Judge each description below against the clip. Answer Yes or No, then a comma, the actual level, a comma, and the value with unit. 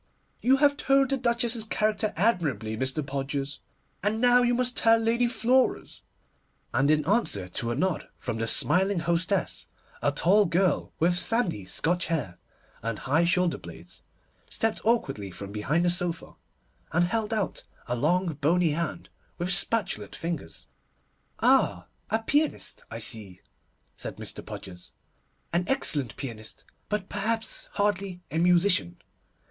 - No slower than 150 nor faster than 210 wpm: No, average, 140 wpm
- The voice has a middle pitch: Yes, medium, 175 Hz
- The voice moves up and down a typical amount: No, wide, 8.1 semitones